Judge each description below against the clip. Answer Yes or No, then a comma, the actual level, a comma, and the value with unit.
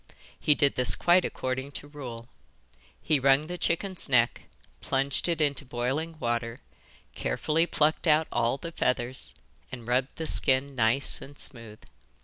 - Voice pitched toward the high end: No, low, 135 Hz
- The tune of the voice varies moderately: Yes, average, 4.0 semitones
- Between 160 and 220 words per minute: No, average, 145 wpm